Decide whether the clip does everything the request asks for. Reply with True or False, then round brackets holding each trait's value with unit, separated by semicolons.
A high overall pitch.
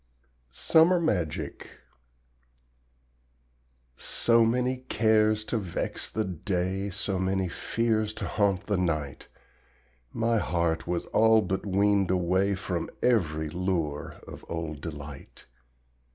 False (95 Hz)